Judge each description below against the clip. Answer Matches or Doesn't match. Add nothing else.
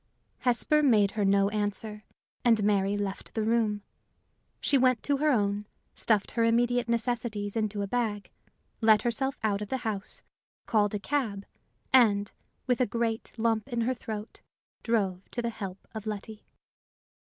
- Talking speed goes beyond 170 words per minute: Doesn't match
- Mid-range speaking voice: Doesn't match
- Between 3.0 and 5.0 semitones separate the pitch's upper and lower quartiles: Doesn't match